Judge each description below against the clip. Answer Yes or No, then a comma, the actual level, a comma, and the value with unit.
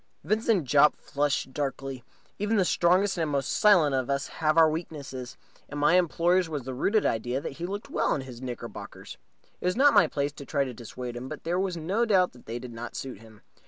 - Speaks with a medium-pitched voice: Yes, medium, 145 Hz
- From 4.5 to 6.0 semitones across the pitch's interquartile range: Yes, wide, 5.6 semitones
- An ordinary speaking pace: No, fast, 215 wpm